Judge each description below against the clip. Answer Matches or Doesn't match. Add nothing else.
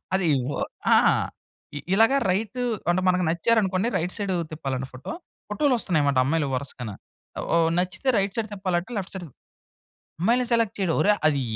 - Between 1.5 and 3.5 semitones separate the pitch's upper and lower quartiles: Doesn't match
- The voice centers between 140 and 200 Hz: Matches